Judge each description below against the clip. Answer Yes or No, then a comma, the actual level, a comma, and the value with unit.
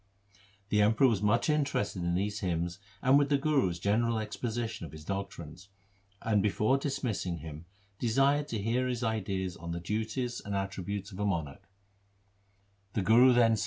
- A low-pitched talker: Yes, low, 105 Hz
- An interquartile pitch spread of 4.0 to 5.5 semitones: Yes, average, 4.3 semitones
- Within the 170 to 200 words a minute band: No, average, 155 wpm